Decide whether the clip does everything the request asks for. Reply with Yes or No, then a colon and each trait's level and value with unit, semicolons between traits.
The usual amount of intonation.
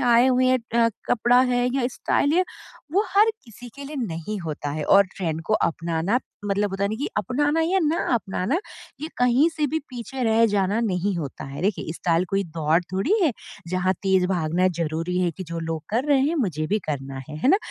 No: wide, 7.2 semitones